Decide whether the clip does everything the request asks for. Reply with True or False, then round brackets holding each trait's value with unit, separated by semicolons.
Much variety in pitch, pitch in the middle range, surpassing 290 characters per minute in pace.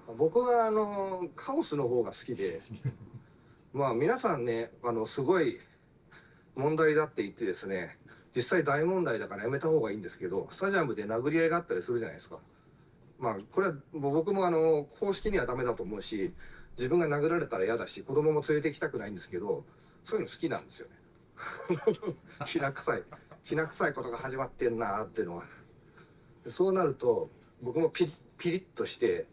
True (8.7 semitones; 170 Hz; 370 characters per minute)